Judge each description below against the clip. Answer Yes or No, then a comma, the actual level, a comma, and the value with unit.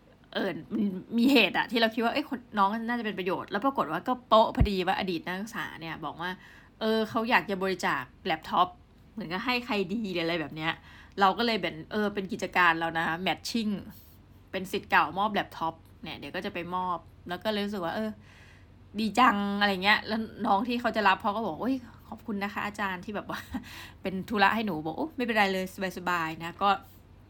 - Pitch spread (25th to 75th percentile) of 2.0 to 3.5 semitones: No, average, 4.0 semitones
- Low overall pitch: No, high, 195 Hz